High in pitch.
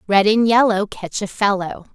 Yes: high, 205 Hz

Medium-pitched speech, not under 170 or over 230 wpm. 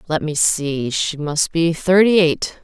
No: medium, 160 Hz; average, 160 wpm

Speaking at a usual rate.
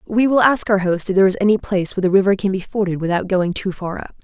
No: fast, 300 wpm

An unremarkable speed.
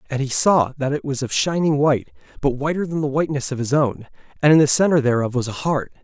No: fast, 250 wpm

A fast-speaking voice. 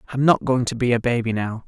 Yes: fast, 285 wpm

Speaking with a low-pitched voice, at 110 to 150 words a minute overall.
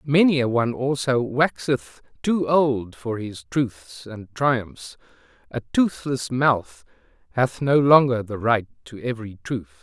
Yes: low, 120 Hz; average, 140 wpm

